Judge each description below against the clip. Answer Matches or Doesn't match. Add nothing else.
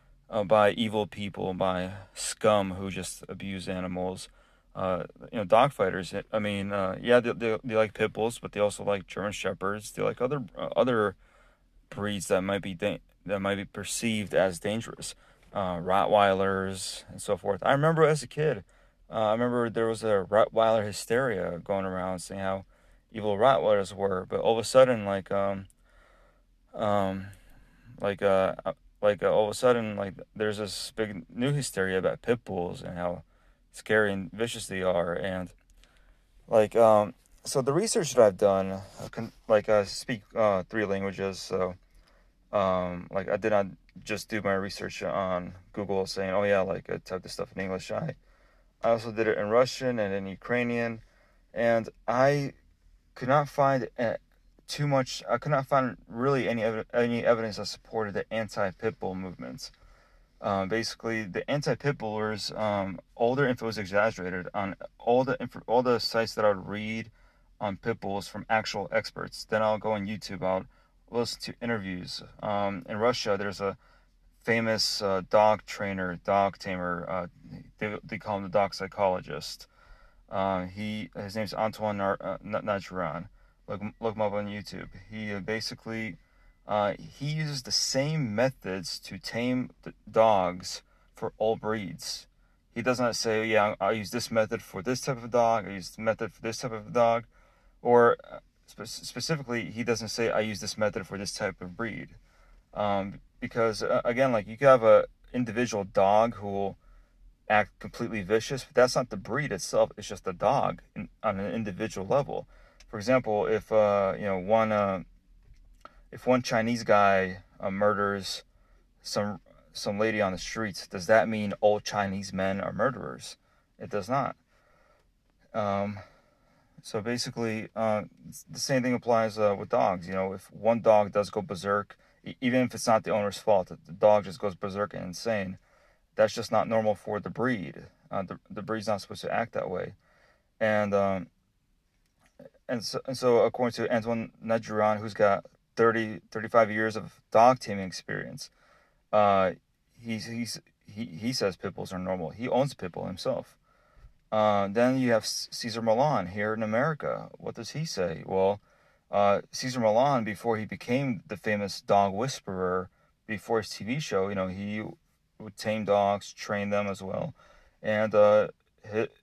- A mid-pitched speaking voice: Doesn't match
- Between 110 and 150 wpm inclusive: Doesn't match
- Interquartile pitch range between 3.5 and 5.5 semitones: Doesn't match